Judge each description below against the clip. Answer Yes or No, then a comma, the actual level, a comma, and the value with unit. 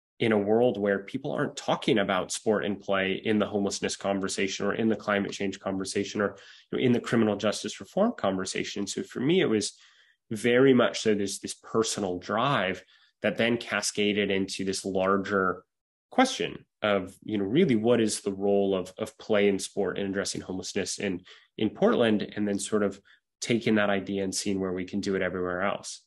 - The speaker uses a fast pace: No, average, 190 wpm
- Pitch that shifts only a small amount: Yes, narrow, 1.2 semitones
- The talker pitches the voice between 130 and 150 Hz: No, low, 100 Hz